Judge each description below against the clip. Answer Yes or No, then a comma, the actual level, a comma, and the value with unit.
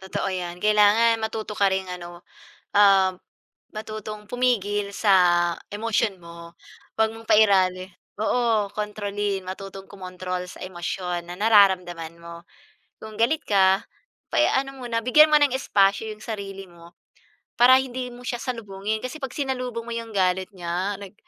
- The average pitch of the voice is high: Yes, high, 205 Hz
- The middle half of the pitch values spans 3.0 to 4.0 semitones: Yes, average, 3.6 semitones